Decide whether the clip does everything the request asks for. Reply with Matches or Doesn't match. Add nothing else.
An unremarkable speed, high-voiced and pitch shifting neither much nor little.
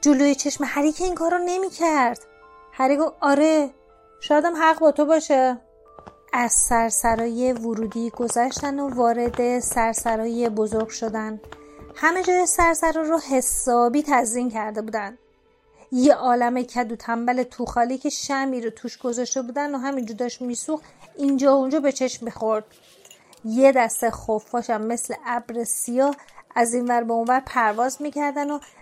Matches